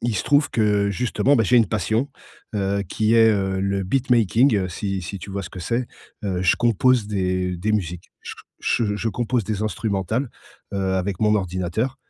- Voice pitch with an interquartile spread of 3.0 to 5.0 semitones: Yes, average, 3.4 semitones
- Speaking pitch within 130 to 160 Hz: No, low, 105 Hz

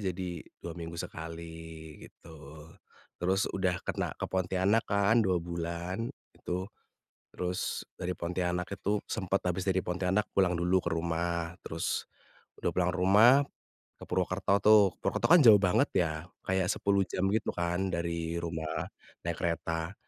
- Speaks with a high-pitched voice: No, very low, 90 Hz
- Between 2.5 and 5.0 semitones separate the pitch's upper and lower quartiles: No, narrow, 2.1 semitones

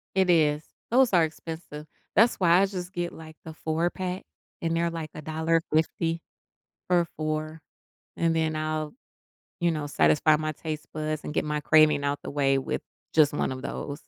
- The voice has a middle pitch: Yes, medium, 160 Hz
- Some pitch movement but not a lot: No, narrow, 1.8 semitones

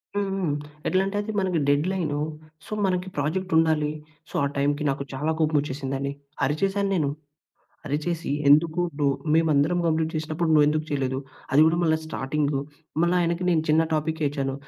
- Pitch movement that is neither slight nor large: Yes, average, 3.1 semitones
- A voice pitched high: No, medium, 155 Hz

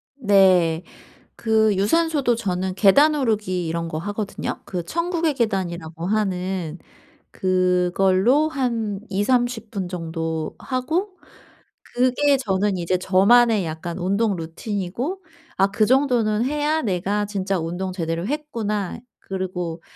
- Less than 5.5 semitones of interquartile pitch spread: Yes, average, 5.1 semitones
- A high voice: Yes, high, 200 Hz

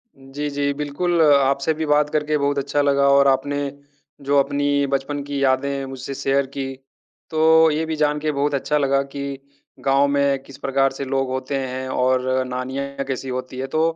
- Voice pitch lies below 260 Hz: Yes, medium, 140 Hz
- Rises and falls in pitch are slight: Yes, narrow, 1.2 semitones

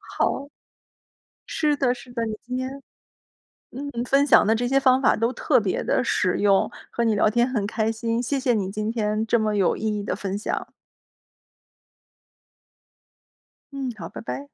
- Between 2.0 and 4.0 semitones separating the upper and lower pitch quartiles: Yes, average, 3.5 semitones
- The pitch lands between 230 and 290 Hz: Yes, high, 235 Hz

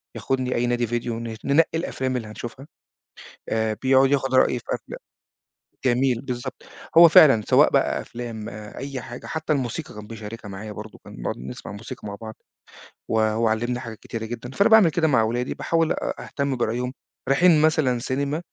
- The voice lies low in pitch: Yes, low, 120 Hz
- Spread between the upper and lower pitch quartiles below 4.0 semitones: Yes, average, 3.6 semitones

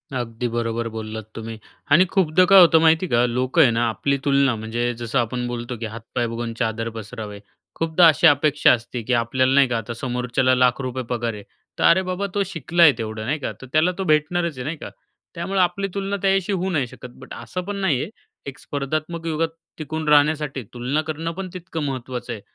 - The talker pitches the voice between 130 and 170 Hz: Yes, low, 135 Hz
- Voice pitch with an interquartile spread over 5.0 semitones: Yes, wide, 5.6 semitones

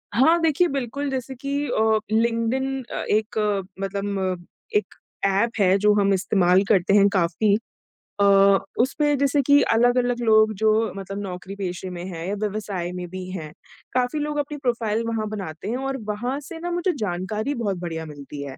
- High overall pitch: Yes, high, 215 Hz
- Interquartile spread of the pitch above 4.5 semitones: Yes, wide, 5.6 semitones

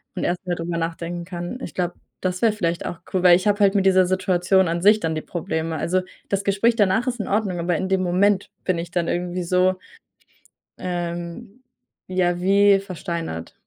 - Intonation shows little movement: Yes, narrow, 2.2 semitones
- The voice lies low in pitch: No, medium, 180 Hz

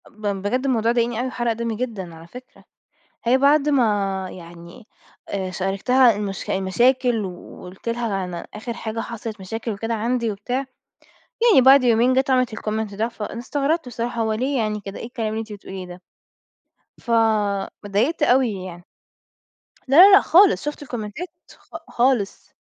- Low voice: No, high, 230 Hz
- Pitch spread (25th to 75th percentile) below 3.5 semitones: No, average, 4.0 semitones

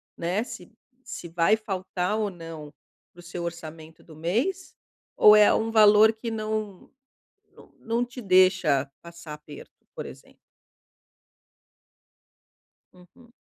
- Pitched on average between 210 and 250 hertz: No, medium, 185 Hz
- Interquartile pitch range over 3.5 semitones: Yes, average, 4.4 semitones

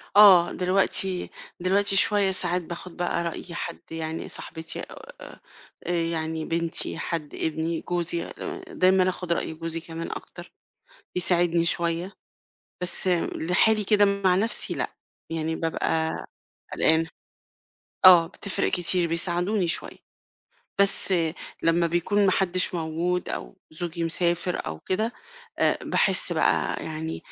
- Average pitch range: No, narrow, 2.2 semitones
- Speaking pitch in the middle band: Yes, medium, 175 Hz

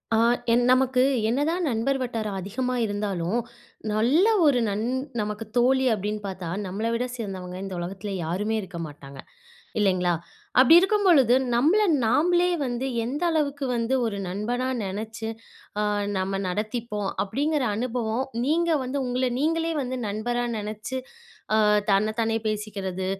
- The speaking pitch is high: Yes, high, 225 Hz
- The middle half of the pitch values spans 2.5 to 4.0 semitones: No, average, 4.5 semitones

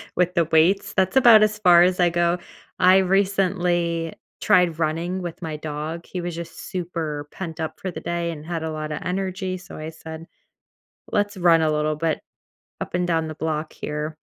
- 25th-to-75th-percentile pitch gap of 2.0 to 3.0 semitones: Yes, narrow, 2.4 semitones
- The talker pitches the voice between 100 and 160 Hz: No, medium, 170 Hz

